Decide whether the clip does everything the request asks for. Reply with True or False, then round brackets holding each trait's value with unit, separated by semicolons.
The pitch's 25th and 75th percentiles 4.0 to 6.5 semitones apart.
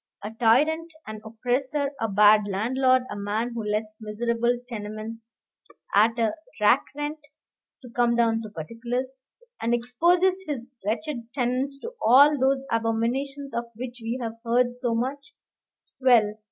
False (2.9 semitones)